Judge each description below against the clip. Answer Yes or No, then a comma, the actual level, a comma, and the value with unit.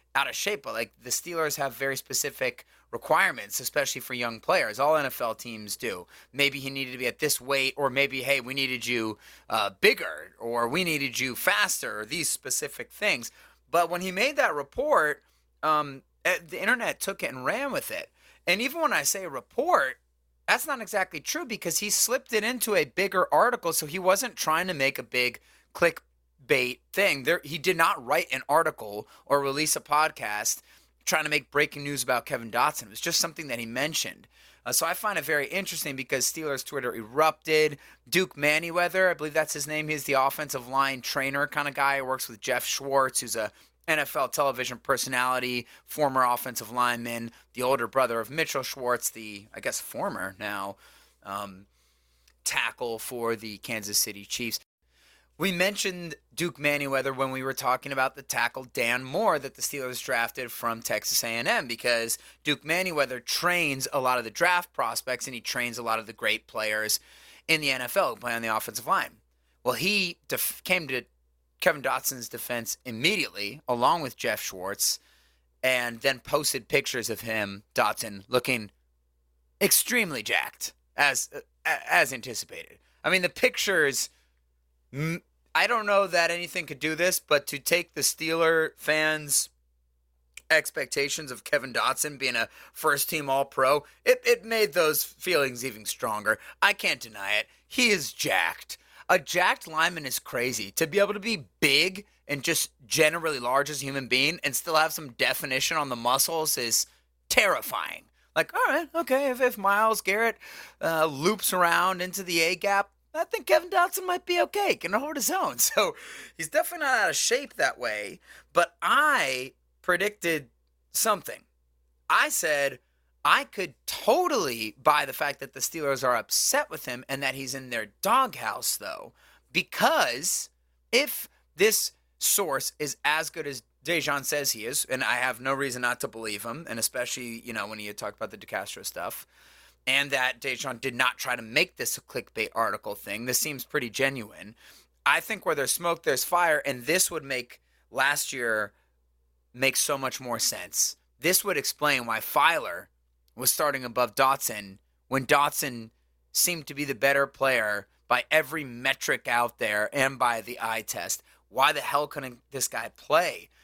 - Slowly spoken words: No, average, 175 wpm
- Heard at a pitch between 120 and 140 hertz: Yes, low, 135 Hz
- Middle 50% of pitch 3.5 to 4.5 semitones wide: No, average, 5.3 semitones